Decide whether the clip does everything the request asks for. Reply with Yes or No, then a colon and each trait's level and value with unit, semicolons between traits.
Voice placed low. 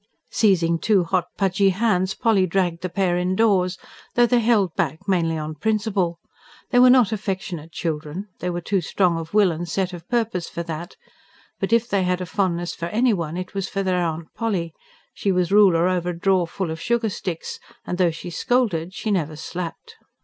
No: medium, 185 Hz